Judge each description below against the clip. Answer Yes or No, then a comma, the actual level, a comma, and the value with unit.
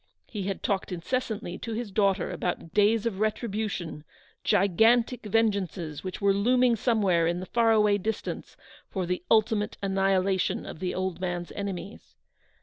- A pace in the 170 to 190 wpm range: No, average, 150 wpm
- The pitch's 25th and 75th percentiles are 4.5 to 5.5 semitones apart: No, average, 3.2 semitones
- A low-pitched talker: No, high, 200 Hz